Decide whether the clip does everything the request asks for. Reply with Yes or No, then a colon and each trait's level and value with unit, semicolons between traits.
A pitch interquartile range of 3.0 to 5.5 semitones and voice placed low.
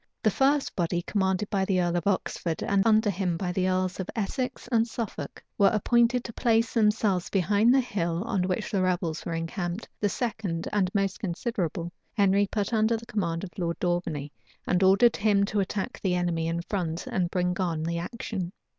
No: average, 3.5 semitones; high, 190 Hz